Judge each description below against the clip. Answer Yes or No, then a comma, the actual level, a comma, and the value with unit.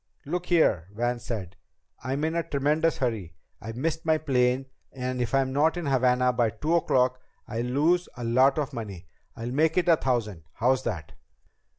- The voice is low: Yes, low, 130 Hz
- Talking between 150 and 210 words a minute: Yes, average, 180 wpm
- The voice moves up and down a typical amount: Yes, average, 4.5 semitones